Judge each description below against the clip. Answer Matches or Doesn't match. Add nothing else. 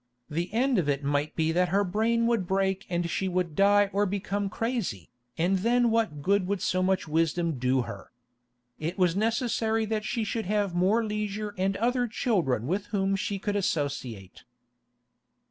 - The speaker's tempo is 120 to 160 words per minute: Doesn't match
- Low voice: Doesn't match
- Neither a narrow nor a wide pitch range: Matches